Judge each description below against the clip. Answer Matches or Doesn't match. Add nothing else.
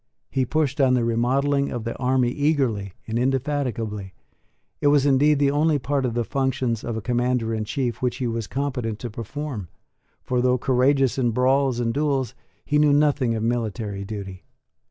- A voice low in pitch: Matches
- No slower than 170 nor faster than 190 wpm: Matches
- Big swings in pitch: Doesn't match